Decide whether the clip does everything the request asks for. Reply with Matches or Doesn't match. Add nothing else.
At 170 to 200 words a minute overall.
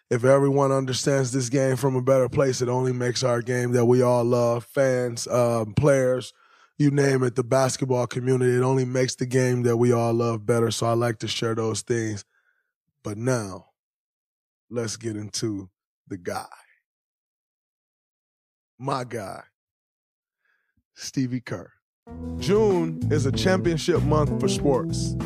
Doesn't match